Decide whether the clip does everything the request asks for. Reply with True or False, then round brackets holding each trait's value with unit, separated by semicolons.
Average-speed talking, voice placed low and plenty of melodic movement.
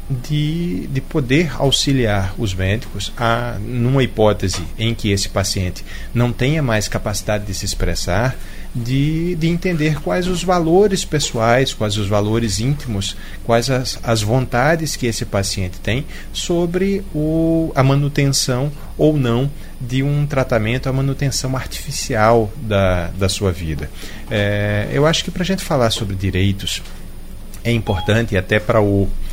True (145 wpm; 115 Hz; 5.8 semitones)